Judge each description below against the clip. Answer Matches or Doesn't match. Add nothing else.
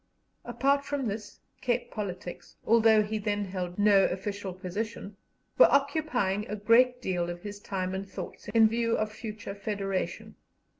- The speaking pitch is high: Matches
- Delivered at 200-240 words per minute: Doesn't match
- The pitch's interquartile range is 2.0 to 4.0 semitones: Matches